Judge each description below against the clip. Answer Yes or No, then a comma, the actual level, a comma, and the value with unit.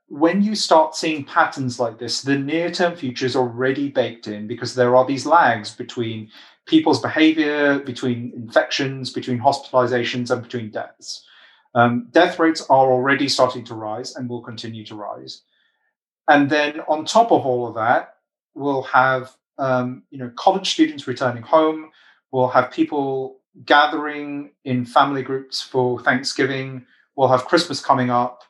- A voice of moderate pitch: No, low, 130 Hz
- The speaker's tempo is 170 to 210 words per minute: No, average, 155 wpm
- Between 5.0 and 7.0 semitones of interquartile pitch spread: No, average, 3.2 semitones